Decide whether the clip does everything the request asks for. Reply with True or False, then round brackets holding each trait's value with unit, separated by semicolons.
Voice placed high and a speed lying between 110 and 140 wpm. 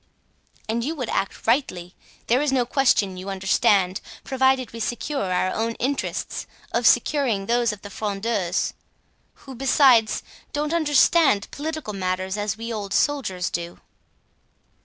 True (230 Hz; 135 wpm)